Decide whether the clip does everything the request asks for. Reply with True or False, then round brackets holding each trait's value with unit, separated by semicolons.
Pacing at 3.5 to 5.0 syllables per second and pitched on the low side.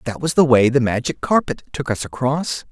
False (5.3 syllables/s; 130 Hz)